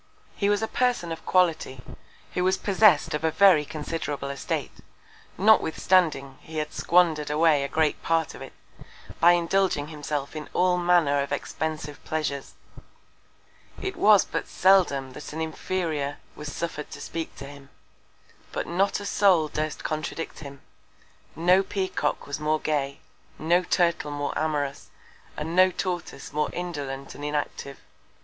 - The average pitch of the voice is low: No, medium, 160 Hz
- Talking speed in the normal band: Yes, average, 145 wpm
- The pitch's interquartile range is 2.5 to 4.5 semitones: Yes, average, 3.5 semitones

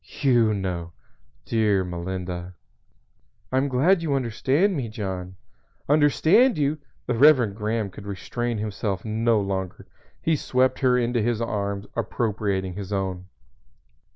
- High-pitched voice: No, low, 110 Hz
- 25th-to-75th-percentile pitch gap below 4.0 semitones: No, average, 5.1 semitones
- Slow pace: Yes, slow, 125 wpm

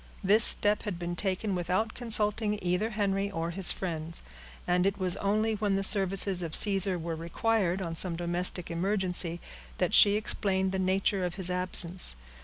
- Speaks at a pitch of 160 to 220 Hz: Yes, high, 190 Hz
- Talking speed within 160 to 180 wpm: Yes, average, 170 wpm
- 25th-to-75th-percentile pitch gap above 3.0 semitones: No, narrow, 2.6 semitones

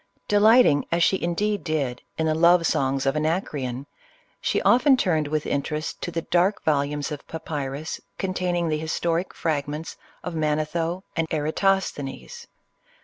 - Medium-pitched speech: Yes, medium, 160 Hz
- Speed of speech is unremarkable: Yes, average, 150 wpm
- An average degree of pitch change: Yes, average, 3.2 semitones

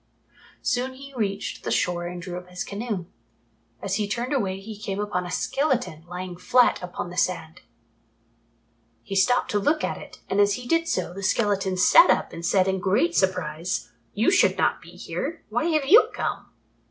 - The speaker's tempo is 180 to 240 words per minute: Yes, average, 190 wpm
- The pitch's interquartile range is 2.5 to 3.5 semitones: No, wide, 5.4 semitones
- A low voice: No, high, 195 Hz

